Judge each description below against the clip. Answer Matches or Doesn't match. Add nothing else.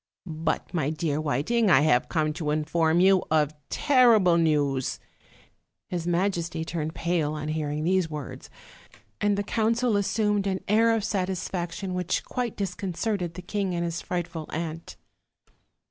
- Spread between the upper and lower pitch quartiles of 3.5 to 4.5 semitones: Matches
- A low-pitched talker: Doesn't match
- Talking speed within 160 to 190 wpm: Doesn't match